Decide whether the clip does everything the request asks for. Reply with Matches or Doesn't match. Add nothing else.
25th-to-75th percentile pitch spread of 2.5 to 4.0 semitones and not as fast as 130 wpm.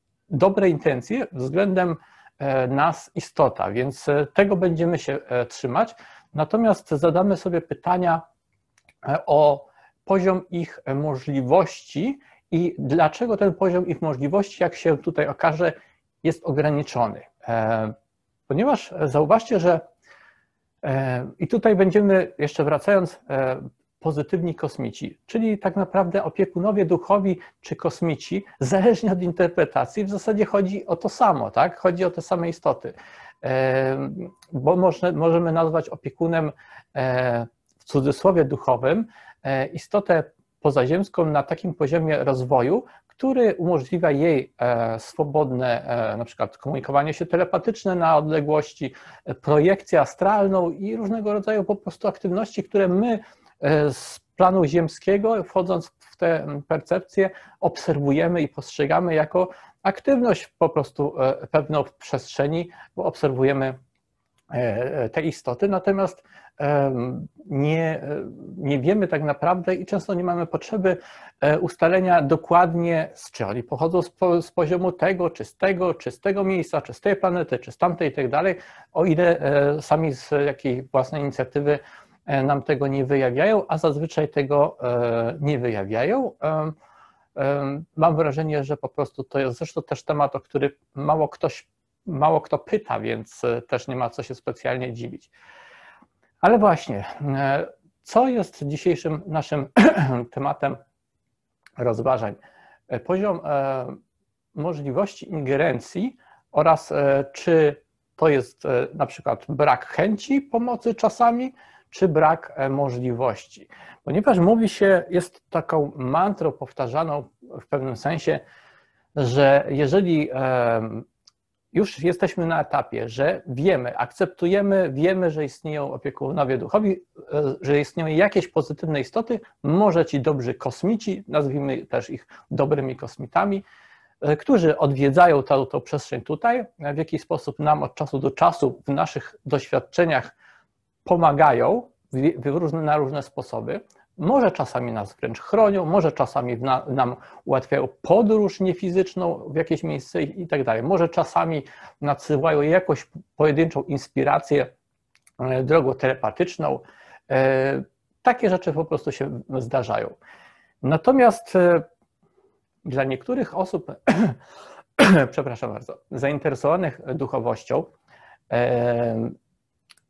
Doesn't match